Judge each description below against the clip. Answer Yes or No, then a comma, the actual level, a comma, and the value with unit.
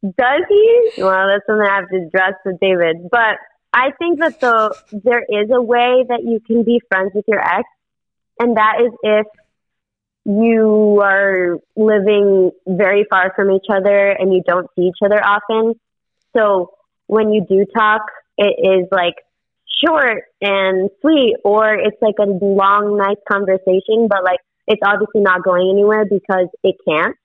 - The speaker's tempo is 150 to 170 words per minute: Yes, average, 165 wpm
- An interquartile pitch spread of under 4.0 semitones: Yes, narrow, 2.4 semitones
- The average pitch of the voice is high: Yes, high, 205 Hz